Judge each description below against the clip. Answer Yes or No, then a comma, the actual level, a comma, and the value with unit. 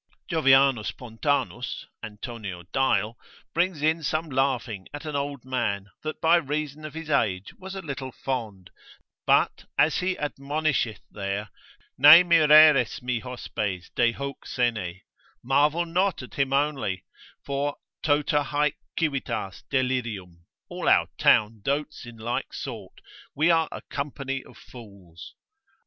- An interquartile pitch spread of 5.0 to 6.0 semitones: Yes, average, 5.3 semitones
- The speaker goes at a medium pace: No, slow, 130 wpm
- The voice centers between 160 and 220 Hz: No, low, 135 Hz